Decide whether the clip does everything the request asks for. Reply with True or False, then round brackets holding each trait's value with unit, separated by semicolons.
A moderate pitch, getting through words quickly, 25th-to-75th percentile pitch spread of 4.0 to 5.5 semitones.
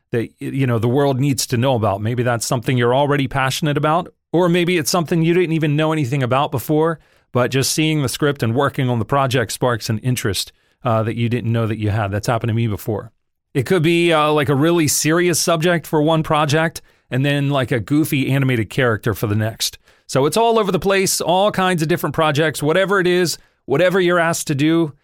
True (145 Hz; 225 wpm; 5.0 semitones)